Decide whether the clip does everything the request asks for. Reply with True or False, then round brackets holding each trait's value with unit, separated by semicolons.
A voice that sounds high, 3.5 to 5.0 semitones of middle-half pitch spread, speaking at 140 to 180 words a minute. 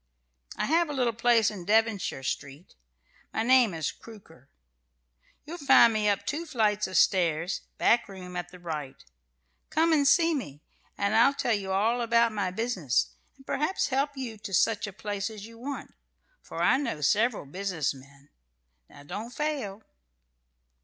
False (215 Hz; 5.5 semitones; 165 wpm)